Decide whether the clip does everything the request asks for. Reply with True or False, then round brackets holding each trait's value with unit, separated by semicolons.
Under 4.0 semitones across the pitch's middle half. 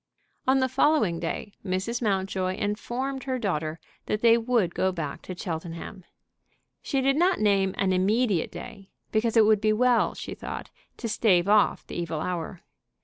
False (4.4 semitones)